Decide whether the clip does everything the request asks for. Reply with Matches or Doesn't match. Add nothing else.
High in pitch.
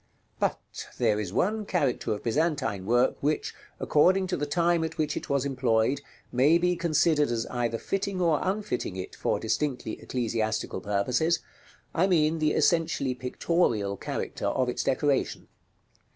Doesn't match